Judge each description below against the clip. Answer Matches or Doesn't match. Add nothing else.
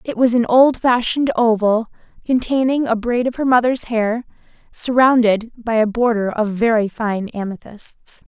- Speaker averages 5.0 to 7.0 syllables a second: Doesn't match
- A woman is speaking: Matches